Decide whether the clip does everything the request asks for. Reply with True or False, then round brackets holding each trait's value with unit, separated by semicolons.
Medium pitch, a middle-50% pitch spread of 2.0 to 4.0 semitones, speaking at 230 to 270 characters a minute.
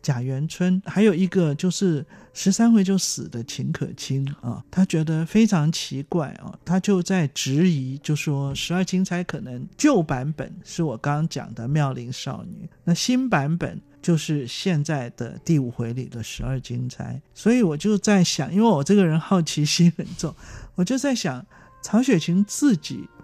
False (165 Hz; 5.2 semitones; 250 characters per minute)